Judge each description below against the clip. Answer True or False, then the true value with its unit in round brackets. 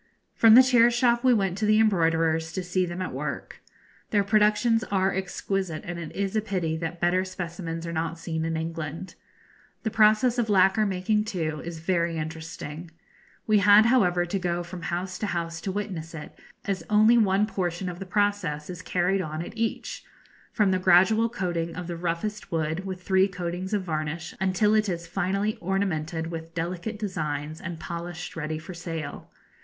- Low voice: False (180 Hz)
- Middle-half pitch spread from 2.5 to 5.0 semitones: True (3.6 semitones)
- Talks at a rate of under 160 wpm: False (180 wpm)